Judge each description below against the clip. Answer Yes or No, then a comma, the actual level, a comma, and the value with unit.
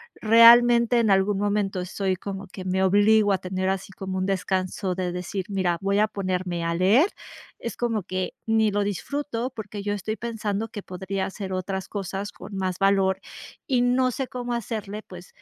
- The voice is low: No, high, 200 Hz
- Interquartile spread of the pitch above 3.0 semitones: No, average, 2.7 semitones